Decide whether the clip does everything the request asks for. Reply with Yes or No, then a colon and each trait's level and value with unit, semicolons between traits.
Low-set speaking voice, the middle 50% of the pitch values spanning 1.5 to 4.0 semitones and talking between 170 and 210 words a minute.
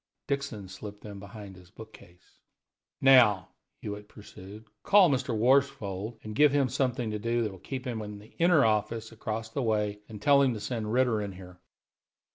Yes: low, 110 Hz; average, 3.7 semitones; average, 180 wpm